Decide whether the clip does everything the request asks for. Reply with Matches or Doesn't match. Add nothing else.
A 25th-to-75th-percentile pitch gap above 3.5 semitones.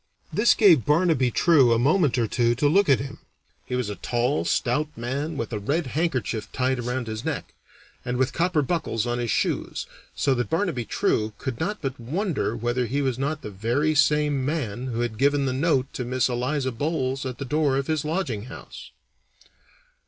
Matches